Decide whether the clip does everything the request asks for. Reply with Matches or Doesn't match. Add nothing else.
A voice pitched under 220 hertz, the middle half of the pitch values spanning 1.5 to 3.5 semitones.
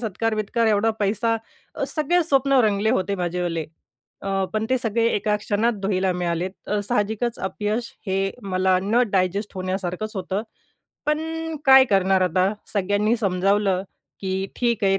Matches